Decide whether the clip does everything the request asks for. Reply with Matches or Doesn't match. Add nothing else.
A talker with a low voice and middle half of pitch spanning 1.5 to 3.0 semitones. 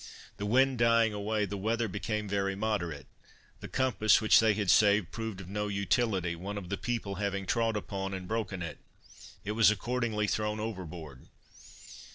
Matches